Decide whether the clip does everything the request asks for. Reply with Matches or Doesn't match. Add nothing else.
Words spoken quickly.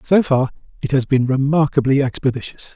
Doesn't match